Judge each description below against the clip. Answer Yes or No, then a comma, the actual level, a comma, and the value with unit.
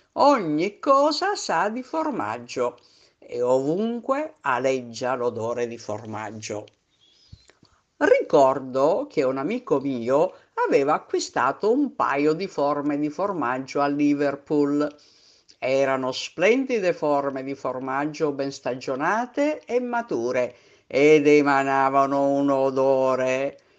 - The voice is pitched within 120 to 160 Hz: Yes, medium, 140 Hz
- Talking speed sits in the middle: No, slow, 100 wpm